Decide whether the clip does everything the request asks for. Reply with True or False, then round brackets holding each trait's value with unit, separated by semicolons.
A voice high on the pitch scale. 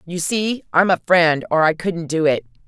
False (170 Hz)